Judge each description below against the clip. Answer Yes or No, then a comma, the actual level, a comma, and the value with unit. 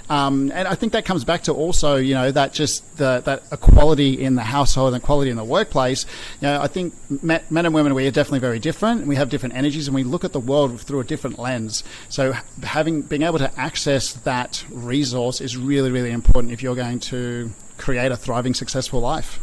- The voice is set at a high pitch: No, low, 135 Hz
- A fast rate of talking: Yes, fast, 220 wpm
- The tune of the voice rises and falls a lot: No, average, 2.9 semitones